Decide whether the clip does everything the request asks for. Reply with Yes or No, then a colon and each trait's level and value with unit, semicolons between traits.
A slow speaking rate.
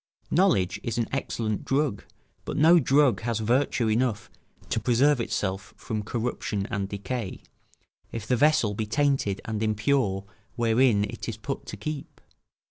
No: average, 145 wpm